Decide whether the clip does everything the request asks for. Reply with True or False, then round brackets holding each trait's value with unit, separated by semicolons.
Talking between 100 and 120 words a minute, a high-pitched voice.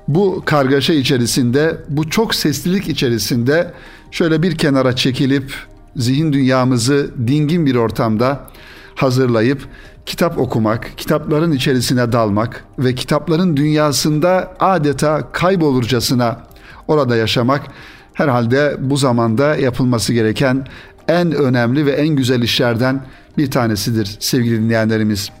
False (105 wpm; 135 Hz)